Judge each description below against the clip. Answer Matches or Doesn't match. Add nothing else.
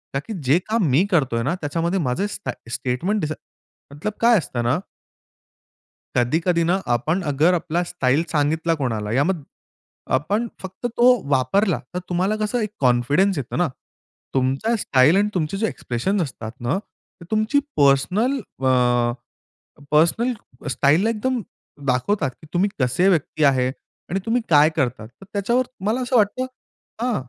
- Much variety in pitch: Matches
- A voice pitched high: Doesn't match